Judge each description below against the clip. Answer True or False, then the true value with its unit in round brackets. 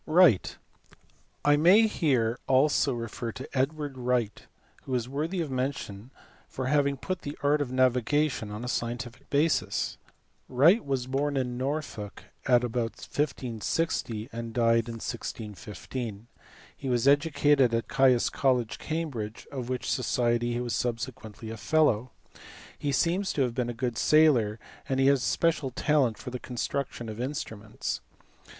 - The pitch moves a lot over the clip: False (3.5 semitones)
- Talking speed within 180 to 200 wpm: False (150 wpm)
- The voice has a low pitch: True (130 Hz)